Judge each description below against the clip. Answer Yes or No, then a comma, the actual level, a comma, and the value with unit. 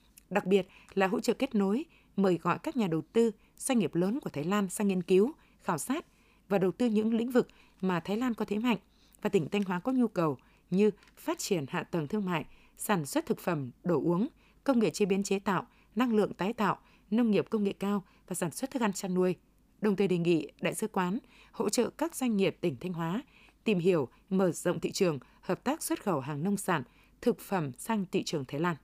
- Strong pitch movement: No, average, 3.9 semitones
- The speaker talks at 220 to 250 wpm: Yes, average, 235 wpm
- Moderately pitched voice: No, high, 200 Hz